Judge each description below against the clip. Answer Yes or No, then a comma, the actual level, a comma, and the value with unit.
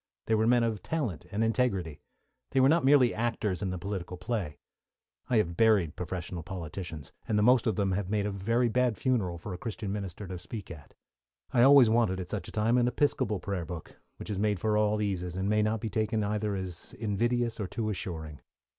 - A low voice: Yes, low, 105 Hz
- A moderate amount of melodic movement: Yes, average, 3.9 semitones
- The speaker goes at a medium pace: No, fast, 210 wpm